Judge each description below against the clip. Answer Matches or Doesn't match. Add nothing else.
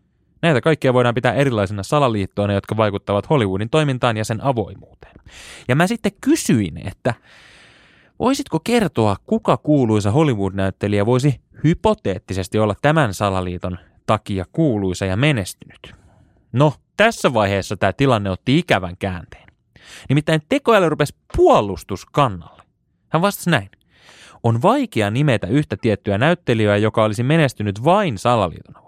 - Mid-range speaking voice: Doesn't match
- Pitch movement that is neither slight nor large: Doesn't match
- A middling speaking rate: Matches